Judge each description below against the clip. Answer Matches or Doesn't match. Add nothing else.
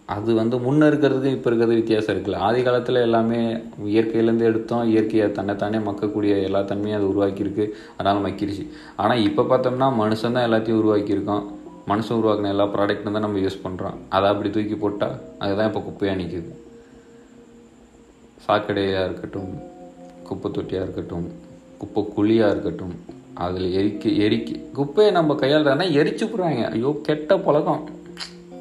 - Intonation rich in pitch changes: Doesn't match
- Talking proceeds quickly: Matches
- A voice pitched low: Matches